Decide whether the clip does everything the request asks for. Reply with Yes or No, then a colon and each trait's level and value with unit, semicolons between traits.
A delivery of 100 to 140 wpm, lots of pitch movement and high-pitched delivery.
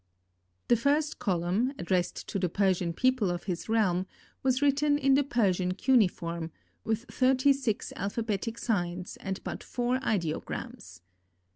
Yes: slow, 135 wpm; wide, 6.2 semitones; high, 215 Hz